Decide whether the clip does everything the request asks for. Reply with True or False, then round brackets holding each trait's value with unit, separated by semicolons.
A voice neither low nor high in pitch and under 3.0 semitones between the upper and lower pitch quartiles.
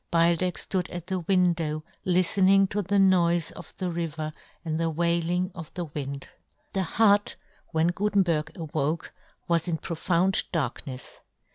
True (170 Hz; 2.4 semitones)